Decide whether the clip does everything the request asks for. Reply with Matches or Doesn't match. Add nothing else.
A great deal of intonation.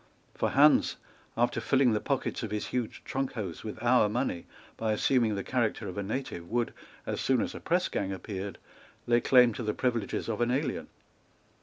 Doesn't match